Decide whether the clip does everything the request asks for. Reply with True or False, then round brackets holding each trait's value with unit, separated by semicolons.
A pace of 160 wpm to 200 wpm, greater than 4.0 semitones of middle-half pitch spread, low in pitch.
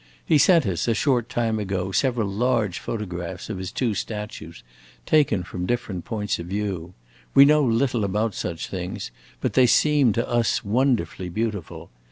True (165 wpm; 4.7 semitones; 105 Hz)